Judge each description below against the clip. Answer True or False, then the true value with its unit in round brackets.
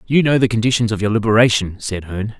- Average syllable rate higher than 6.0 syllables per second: True (6.8 syllables/s)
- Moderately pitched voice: False (110 Hz)